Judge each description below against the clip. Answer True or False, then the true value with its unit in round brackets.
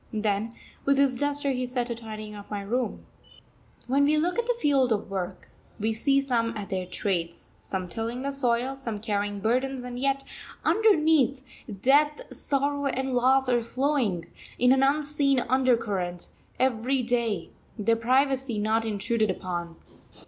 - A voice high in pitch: True (245 Hz)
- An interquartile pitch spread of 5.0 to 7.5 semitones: False (4.1 semitones)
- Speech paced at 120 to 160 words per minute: True (155 wpm)